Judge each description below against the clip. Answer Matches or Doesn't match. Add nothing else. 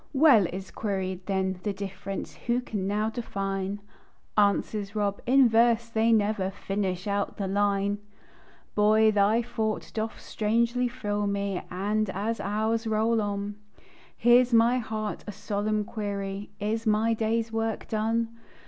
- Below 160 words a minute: Matches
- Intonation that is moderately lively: Doesn't match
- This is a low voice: Doesn't match